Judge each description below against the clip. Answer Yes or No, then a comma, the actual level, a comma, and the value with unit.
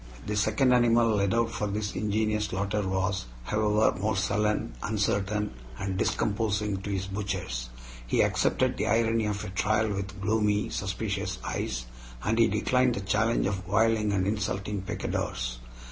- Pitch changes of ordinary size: No, narrow, 1.9 semitones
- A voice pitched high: No, low, 105 Hz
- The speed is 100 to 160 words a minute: Yes, average, 150 wpm